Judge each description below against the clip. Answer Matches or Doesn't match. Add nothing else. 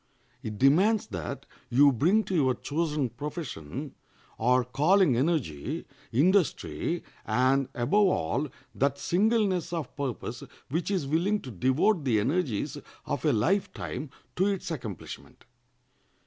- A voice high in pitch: Doesn't match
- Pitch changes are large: Matches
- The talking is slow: Matches